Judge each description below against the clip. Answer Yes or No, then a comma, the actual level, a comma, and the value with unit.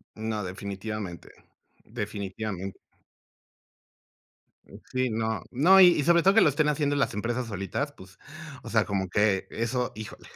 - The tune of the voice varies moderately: No, wide, 5.7 semitones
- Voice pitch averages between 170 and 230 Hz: No, low, 110 Hz